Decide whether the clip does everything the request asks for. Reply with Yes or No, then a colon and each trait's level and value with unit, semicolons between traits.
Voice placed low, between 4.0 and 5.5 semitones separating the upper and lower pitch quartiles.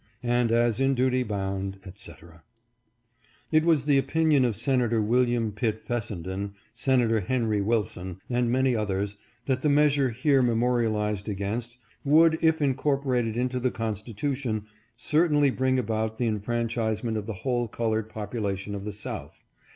No: low, 120 Hz; average, 3.6 semitones